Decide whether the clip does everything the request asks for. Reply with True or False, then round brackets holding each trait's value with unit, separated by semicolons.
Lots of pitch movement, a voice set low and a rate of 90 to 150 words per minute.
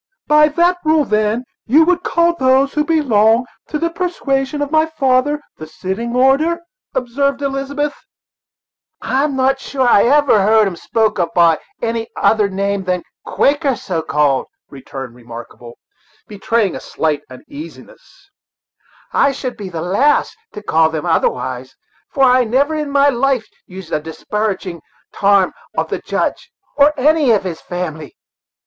False (7.7 semitones; 240 Hz; 145 wpm)